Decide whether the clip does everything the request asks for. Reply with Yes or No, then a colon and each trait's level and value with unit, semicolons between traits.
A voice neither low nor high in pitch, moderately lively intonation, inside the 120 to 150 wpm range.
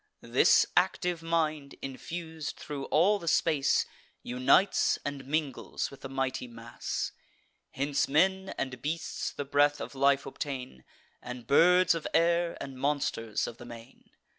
Yes: medium, 145 Hz; average, 3.8 semitones; average, 140 wpm